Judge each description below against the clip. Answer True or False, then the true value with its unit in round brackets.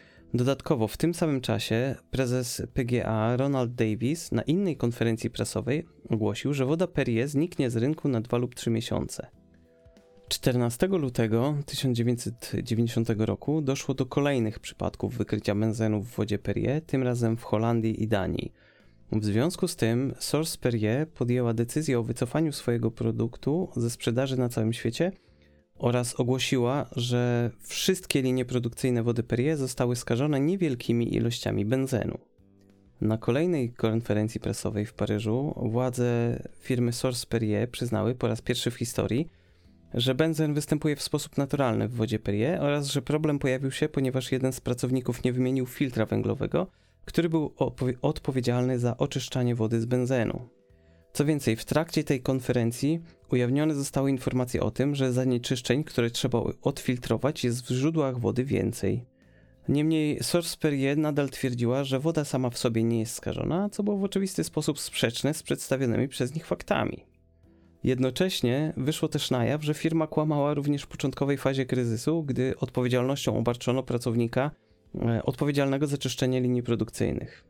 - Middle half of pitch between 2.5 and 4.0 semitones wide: True (3.6 semitones)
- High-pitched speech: False (125 Hz)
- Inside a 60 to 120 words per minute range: False (145 wpm)